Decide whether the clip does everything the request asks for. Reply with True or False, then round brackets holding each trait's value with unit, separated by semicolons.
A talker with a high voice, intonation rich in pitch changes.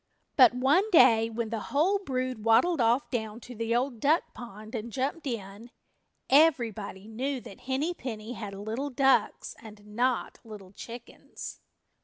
False (235 Hz; 3.6 semitones)